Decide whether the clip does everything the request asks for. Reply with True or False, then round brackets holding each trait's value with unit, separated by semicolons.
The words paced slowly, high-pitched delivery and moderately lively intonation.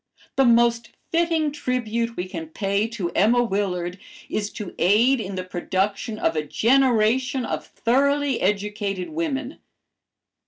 True (130 wpm; 225 Hz; 4.9 semitones)